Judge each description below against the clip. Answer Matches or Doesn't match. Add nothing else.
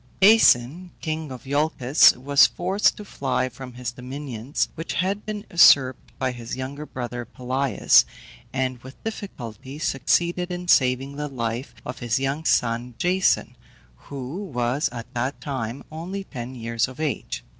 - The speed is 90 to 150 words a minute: Matches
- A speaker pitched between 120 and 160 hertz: Matches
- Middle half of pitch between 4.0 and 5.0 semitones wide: Matches